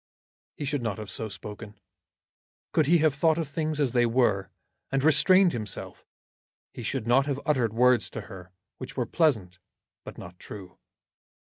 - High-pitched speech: No, low, 125 Hz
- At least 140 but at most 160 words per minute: No, average, 170 wpm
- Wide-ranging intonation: Yes, wide, 5.9 semitones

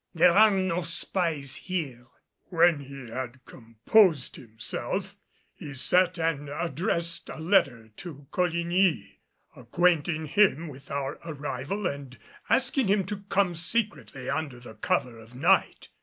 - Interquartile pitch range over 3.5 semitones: Yes, average, 5.2 semitones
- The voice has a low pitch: No, medium, 160 Hz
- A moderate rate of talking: No, slow, 125 wpm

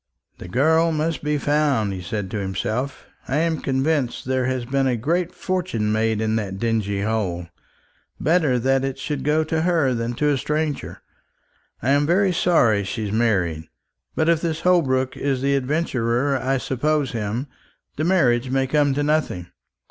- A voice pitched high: No, low, 135 Hz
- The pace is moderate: Yes, average, 165 wpm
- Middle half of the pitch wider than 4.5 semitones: Yes, average, 5.3 semitones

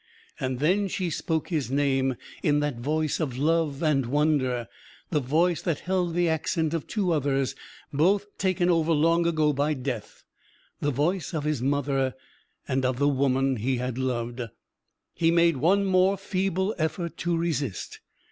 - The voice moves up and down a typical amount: Yes, average, 4.1 semitones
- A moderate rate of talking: Yes, average, 160 wpm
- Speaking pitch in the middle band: Yes, medium, 150 Hz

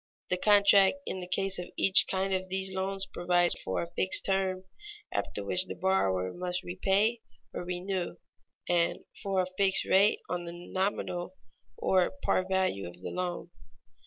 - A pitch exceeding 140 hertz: Yes, medium, 185 Hz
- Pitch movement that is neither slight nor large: No, narrow, 1.4 semitones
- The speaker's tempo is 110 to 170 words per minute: Yes, average, 160 wpm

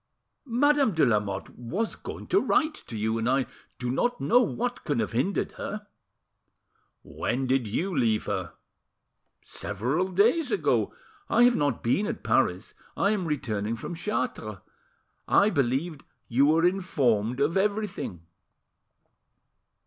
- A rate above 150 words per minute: No, slow, 135 wpm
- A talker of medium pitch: Yes, medium, 145 Hz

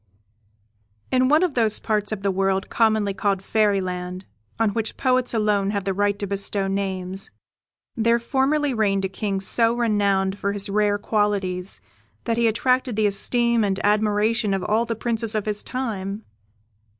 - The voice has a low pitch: No, high, 210 Hz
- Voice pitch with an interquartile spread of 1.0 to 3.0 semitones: Yes, average, 2.7 semitones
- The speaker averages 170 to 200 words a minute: No, average, 160 wpm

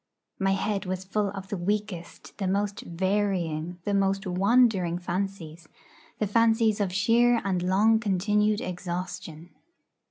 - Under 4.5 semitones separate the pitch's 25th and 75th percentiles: Yes, narrow, 2.6 semitones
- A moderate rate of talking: No, slow, 130 wpm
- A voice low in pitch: No, high, 195 Hz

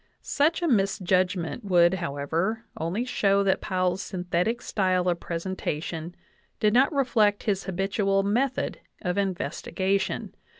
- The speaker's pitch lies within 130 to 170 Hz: No, high, 195 Hz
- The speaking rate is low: Yes, slow, 125 wpm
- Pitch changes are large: No, average, 3.0 semitones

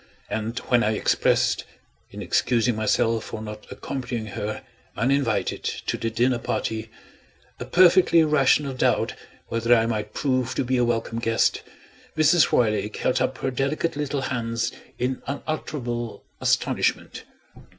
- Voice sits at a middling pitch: No, low, 120 Hz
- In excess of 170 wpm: No, slow, 135 wpm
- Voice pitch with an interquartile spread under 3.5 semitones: Yes, average, 3.1 semitones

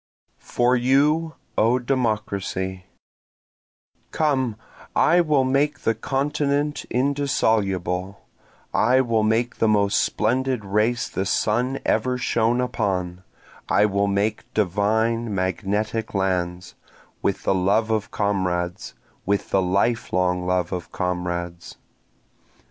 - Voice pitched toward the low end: Yes, low, 105 Hz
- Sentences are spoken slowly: Yes, slow, 110 wpm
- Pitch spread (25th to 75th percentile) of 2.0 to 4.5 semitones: No, average, 5.0 semitones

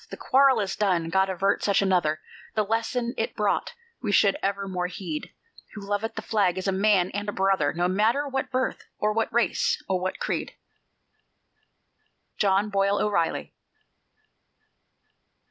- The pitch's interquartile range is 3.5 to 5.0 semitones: No, narrow, 2.4 semitones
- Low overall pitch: No, high, 200 Hz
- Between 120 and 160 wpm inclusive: Yes, average, 150 wpm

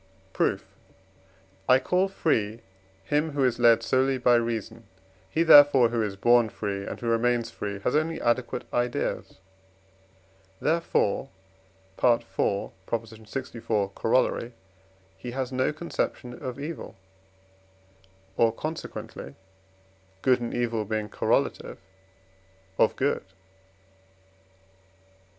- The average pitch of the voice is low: Yes, low, 120 Hz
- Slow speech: Yes, slow, 105 wpm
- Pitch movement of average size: Yes, average, 3.0 semitones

